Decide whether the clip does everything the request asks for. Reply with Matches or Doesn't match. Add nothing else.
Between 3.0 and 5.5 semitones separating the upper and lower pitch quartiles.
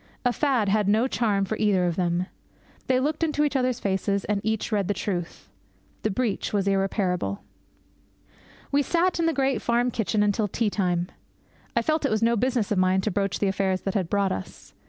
Matches